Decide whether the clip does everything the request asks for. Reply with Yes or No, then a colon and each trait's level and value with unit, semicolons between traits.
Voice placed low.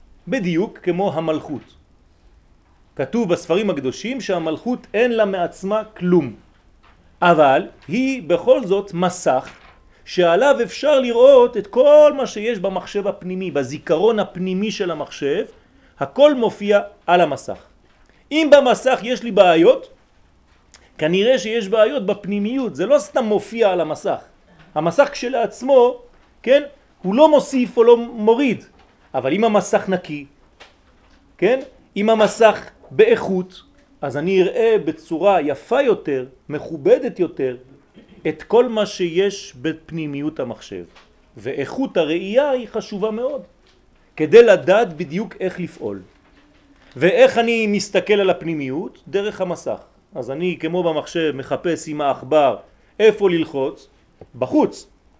No: high, 200 Hz